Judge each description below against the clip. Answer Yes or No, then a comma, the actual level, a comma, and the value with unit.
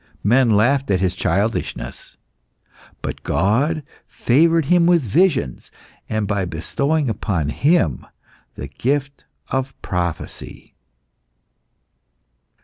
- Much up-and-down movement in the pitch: Yes, wide, 7.0 semitones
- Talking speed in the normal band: No, slow, 95 wpm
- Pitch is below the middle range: Yes, low, 120 Hz